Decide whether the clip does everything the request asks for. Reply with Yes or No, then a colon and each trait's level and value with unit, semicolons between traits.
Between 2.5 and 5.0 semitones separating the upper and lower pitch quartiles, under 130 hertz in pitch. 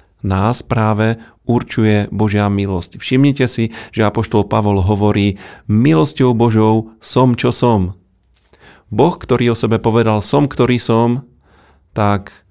Yes: average, 2.8 semitones; low, 110 Hz